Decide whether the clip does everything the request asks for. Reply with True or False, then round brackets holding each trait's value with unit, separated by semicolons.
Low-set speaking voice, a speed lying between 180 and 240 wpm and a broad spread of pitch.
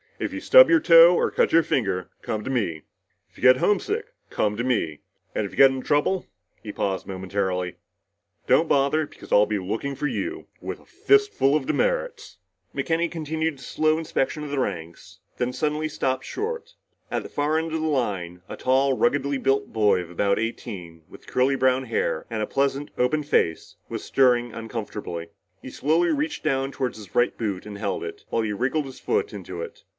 True (130 Hz; 200 wpm; 6.9 semitones)